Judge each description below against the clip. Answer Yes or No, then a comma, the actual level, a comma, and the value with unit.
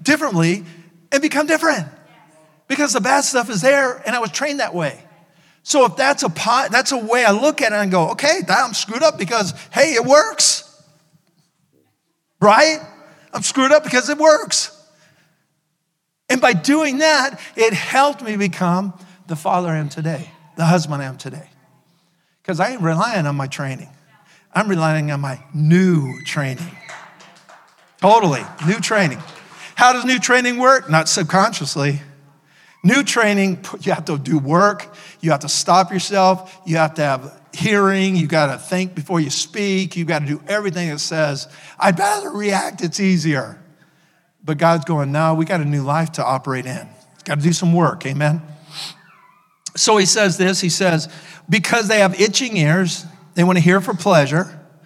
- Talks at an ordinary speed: Yes, average, 175 wpm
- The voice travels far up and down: No, average, 4.8 semitones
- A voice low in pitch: No, medium, 175 Hz